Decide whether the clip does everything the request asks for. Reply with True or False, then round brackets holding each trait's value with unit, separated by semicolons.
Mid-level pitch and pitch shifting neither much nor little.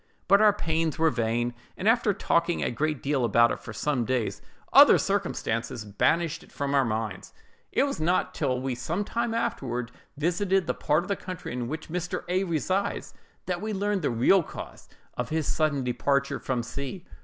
False (155 Hz; 6.8 semitones)